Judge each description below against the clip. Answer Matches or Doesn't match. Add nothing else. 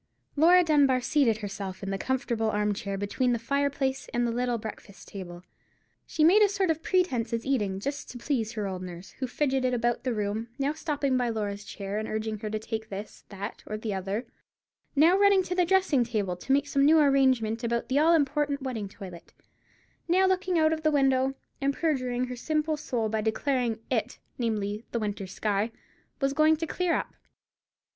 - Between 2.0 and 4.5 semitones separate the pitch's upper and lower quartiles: Doesn't match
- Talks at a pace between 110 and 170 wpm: Doesn't match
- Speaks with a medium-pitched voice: Doesn't match